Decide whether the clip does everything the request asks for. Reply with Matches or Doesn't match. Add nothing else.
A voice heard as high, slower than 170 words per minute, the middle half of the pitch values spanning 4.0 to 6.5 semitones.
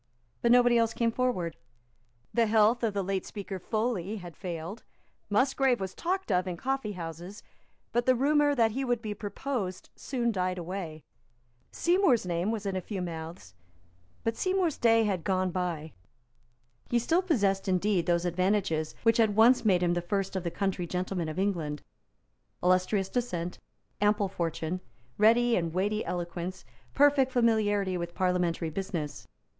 Matches